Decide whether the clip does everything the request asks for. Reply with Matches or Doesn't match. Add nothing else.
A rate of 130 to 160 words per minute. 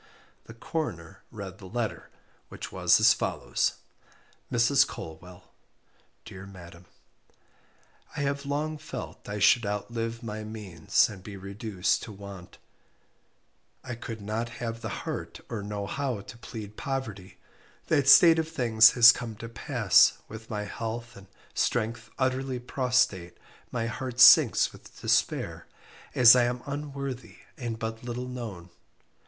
Matches